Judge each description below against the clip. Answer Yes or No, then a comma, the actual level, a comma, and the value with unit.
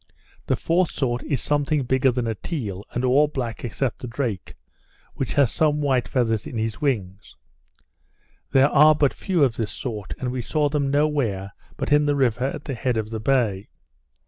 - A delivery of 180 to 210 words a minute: Yes, average, 195 wpm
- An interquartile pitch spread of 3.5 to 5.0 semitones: Yes, average, 4.3 semitones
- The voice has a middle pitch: No, low, 130 Hz